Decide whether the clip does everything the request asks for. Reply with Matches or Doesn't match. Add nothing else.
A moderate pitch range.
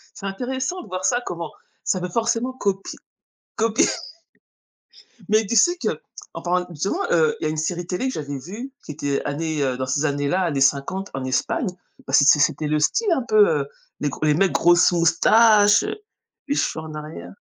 Doesn't match